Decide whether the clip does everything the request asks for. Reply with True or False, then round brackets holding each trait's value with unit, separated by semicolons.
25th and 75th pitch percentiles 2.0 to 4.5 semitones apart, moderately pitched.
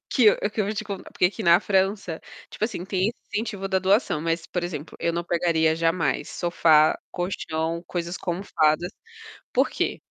True (2.9 semitones; 175 Hz)